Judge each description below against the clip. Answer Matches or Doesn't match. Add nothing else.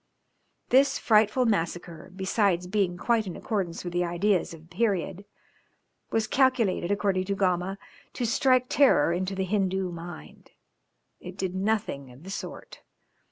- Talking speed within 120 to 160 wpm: Matches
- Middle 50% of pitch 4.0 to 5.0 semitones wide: Doesn't match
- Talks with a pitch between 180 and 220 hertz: Matches